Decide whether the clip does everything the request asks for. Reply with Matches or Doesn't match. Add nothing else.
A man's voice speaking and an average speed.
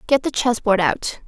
Doesn't match